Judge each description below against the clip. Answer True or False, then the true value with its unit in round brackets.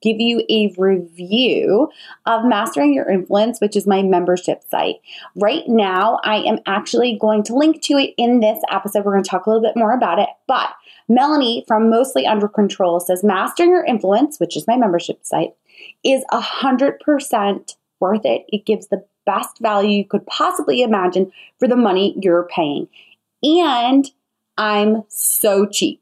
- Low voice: False (215 Hz)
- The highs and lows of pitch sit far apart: False (3.7 semitones)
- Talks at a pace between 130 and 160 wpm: False (170 wpm)